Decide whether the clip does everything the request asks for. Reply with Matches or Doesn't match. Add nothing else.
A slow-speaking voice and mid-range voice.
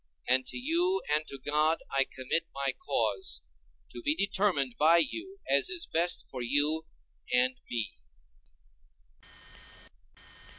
Matches